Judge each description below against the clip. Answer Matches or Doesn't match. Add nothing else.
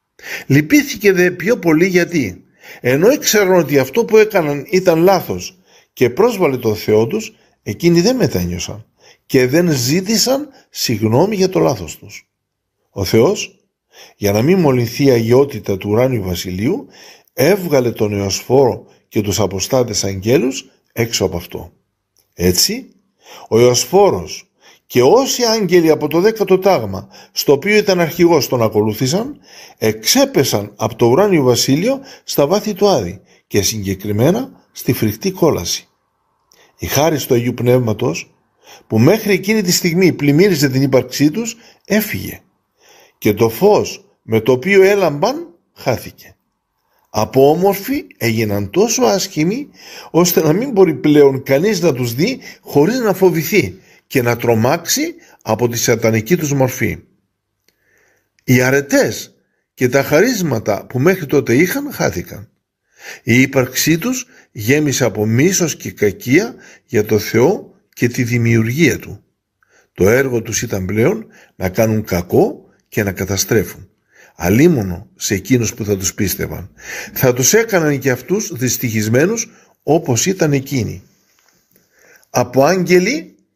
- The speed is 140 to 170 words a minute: Doesn't match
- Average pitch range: Doesn't match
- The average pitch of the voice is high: Doesn't match